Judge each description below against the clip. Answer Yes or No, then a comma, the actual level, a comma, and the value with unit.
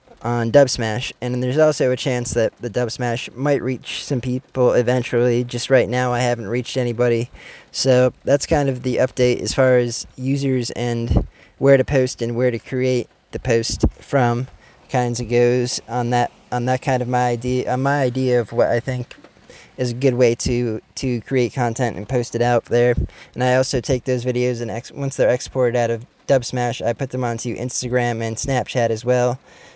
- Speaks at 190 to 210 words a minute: Yes, average, 200 wpm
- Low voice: Yes, low, 125 Hz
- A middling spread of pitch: No, narrow, 1.2 semitones